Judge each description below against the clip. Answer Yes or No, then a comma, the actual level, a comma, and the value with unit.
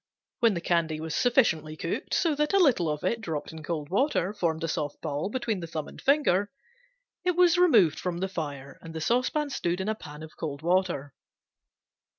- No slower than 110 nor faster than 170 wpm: No, average, 200 wpm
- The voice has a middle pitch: Yes, medium, 175 Hz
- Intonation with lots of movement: Yes, wide, 7.1 semitones